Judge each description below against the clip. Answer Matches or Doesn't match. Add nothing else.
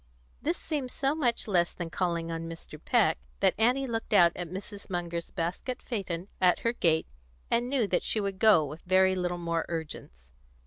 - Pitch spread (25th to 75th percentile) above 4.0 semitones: Matches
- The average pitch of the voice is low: Doesn't match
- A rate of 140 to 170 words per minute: Doesn't match